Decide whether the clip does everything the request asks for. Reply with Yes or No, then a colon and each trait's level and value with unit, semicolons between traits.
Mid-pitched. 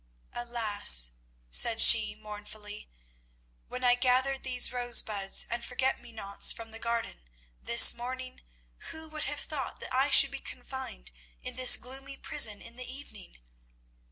No: high, 245 Hz